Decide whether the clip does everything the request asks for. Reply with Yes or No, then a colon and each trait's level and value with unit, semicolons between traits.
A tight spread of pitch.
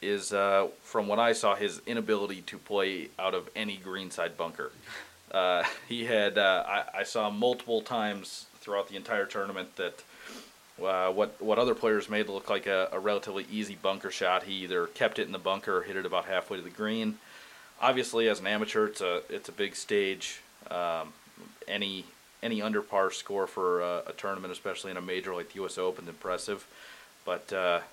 No: average, 3.3 semitones